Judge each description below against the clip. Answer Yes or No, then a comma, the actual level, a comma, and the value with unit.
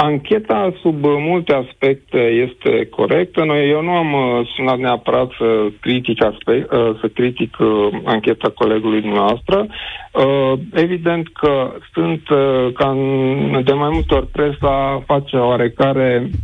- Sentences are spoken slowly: Yes, slow, 105 wpm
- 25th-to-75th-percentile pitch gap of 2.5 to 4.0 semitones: Yes, average, 3.4 semitones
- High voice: No, low, 135 Hz